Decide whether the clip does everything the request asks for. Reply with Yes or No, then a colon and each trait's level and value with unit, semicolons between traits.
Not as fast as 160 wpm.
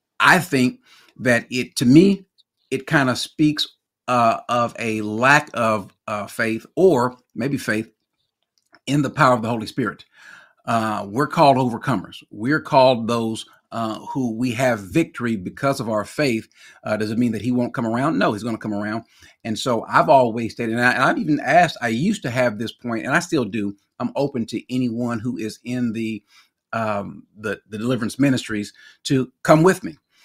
No: average, 190 wpm